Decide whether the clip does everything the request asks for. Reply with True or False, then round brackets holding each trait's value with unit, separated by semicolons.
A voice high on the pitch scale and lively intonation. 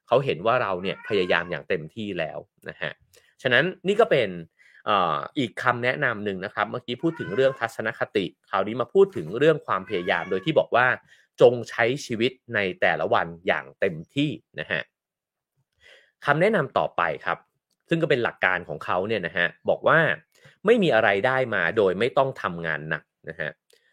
False (125 Hz; 8.2 semitones)